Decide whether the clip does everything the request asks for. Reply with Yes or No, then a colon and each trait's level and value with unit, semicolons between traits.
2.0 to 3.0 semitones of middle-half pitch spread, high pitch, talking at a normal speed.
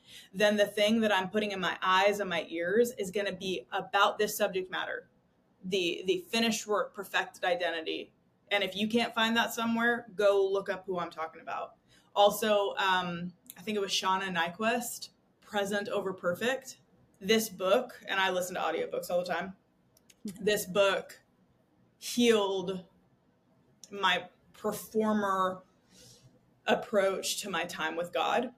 Yes: average, 2.7 semitones; high, 200 Hz; average, 150 wpm